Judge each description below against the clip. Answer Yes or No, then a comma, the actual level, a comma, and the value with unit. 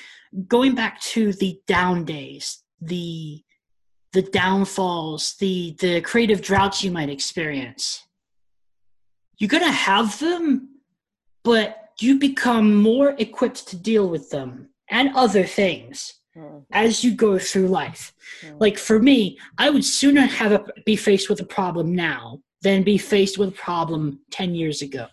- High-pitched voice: Yes, high, 195 Hz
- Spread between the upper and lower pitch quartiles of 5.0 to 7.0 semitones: Yes, wide, 5.4 semitones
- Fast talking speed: No, average, 145 wpm